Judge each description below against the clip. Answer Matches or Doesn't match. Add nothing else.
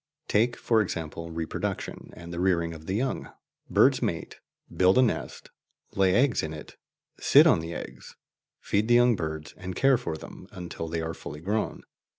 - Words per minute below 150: Doesn't match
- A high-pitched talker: Doesn't match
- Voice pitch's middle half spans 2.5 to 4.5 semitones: Doesn't match